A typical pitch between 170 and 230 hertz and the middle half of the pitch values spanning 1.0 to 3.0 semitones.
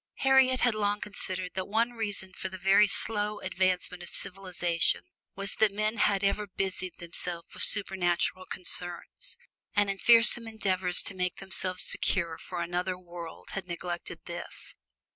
Yes: high, 190 Hz; narrow, 2.6 semitones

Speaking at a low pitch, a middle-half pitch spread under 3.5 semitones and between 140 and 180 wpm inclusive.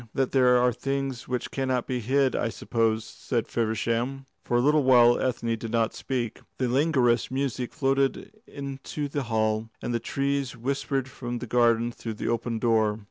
Yes: low, 125 Hz; narrow, 2.6 semitones; average, 175 wpm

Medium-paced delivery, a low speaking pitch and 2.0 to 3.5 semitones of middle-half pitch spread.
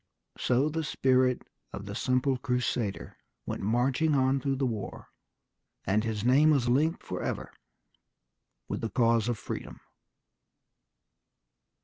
No: slow, 120 wpm; low, 125 Hz; average, 2.7 semitones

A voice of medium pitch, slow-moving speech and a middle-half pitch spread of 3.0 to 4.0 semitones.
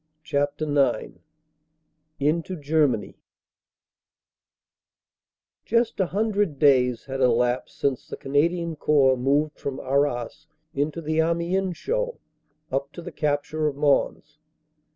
Yes: medium, 150 Hz; slow, 110 wpm; average, 3.5 semitones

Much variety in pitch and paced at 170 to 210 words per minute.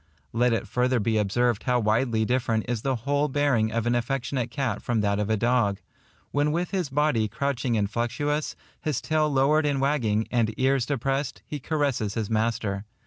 No: average, 4.2 semitones; average, 185 wpm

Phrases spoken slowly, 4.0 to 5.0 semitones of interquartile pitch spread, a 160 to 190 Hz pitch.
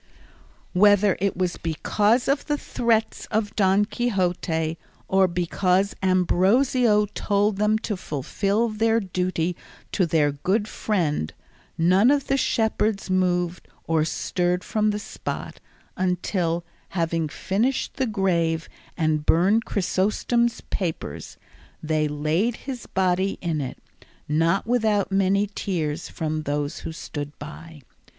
Yes: slow, 120 wpm; average, 4.3 semitones; medium, 185 Hz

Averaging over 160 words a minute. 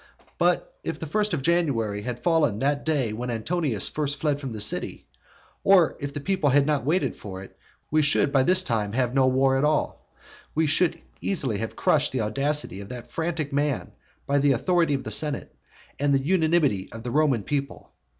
Yes: average, 200 wpm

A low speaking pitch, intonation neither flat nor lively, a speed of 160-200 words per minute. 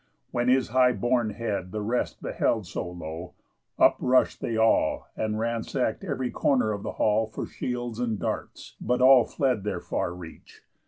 Yes: low, 115 Hz; average, 3.0 semitones; average, 170 wpm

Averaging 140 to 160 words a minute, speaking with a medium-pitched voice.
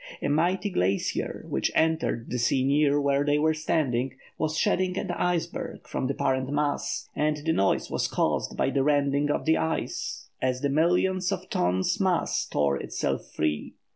No: average, 170 wpm; medium, 145 Hz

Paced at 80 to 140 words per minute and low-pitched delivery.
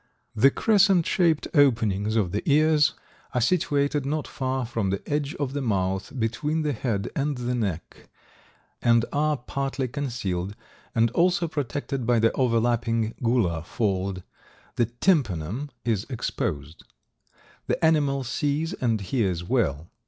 Yes: slow, 135 wpm; low, 120 Hz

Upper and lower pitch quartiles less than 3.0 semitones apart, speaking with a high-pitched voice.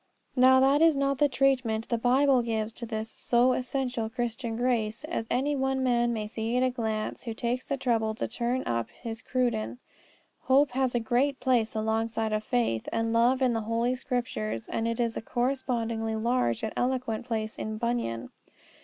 Yes: narrow, 2.4 semitones; high, 240 Hz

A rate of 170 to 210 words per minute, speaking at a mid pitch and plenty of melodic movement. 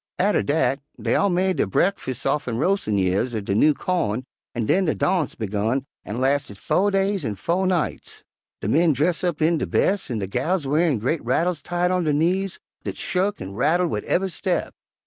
Yes: average, 200 wpm; medium, 155 Hz; wide, 6.8 semitones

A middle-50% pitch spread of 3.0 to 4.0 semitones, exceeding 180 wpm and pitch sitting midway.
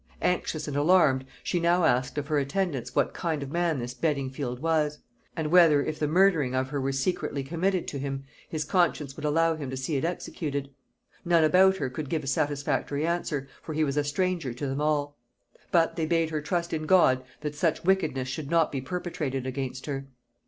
Yes: average, 3.5 semitones; average, 200 wpm; medium, 150 Hz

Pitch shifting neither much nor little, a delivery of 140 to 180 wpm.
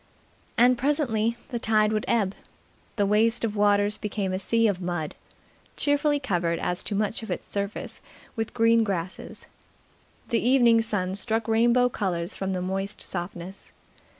Yes: average, 3.3 semitones; average, 150 wpm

